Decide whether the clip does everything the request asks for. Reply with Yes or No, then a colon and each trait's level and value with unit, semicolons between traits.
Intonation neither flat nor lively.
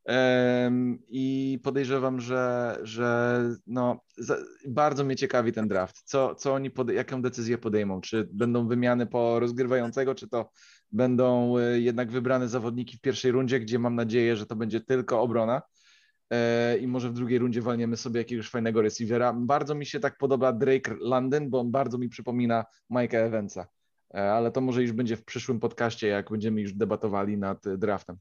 No: narrow, 1.9 semitones